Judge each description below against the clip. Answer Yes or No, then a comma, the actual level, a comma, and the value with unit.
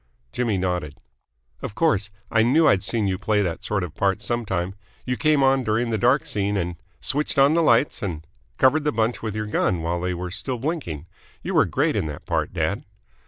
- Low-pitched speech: Yes, low, 105 Hz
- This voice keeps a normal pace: No, fast, 230 wpm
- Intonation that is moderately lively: No, wide, 6.0 semitones